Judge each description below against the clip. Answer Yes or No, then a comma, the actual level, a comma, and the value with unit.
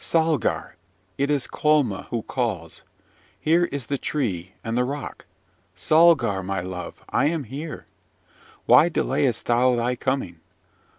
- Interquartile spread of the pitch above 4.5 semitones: Yes, average, 5.1 semitones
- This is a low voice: Yes, low, 130 Hz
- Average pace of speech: No, slow, 130 wpm